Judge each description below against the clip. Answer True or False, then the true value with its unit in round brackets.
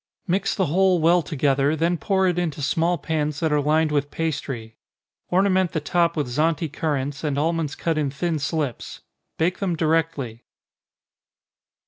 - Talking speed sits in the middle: True (155 wpm)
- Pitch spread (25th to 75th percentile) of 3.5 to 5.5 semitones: False (2.9 semitones)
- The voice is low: False (160 Hz)